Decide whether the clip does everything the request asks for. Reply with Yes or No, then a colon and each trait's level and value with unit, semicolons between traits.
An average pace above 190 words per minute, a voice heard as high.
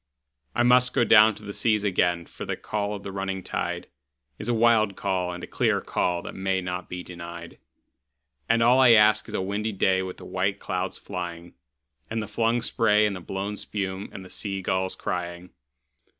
No: average, 200 wpm; low, 100 Hz